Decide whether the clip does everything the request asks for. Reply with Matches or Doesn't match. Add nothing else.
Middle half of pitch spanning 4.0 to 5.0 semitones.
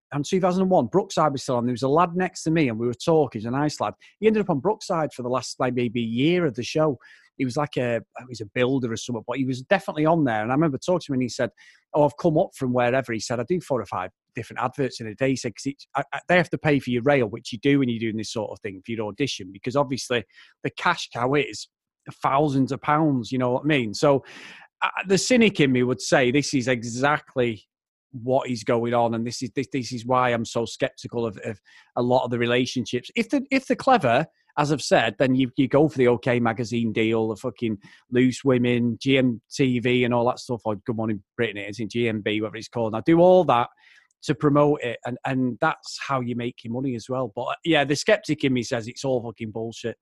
Doesn't match